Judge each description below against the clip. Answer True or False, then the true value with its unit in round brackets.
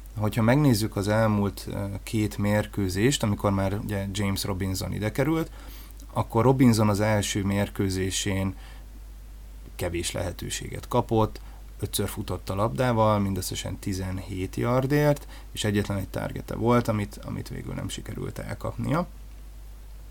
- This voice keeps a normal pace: True (115 wpm)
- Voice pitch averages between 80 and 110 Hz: True (105 Hz)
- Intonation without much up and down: False (3.0 semitones)